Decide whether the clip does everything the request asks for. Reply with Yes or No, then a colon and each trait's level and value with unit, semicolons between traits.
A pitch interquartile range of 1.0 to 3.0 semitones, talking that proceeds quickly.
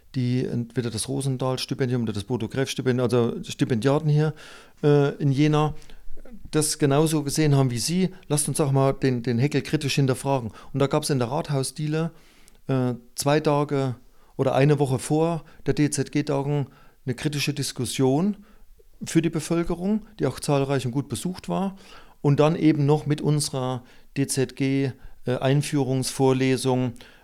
No: average, 2.7 semitones; average, 140 wpm